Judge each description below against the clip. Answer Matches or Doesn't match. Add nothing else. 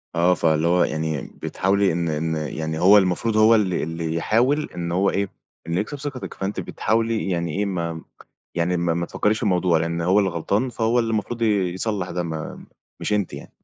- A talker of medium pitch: Doesn't match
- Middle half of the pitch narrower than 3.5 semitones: Doesn't match